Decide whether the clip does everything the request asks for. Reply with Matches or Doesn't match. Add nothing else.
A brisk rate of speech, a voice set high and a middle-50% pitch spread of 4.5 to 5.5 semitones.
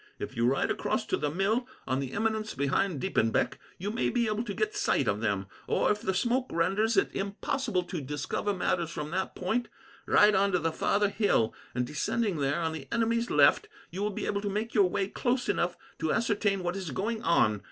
Matches